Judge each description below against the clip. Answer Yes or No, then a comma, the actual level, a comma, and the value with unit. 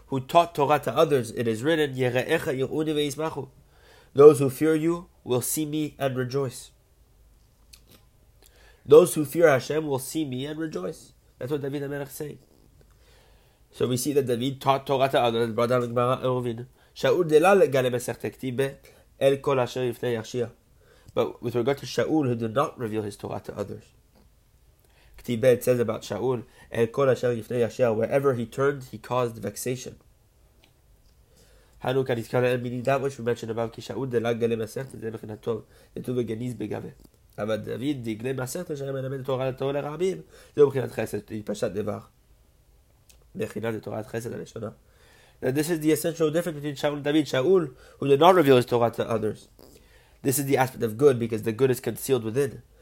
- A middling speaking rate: Yes, average, 160 wpm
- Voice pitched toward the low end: Yes, low, 130 Hz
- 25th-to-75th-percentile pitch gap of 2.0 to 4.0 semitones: Yes, average, 3.4 semitones